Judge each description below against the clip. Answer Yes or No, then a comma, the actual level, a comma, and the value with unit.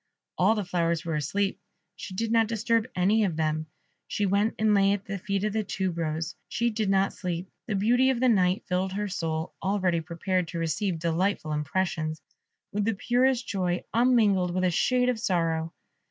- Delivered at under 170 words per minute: No, average, 190 wpm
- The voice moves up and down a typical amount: Yes, average, 4.1 semitones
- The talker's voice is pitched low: No, high, 190 Hz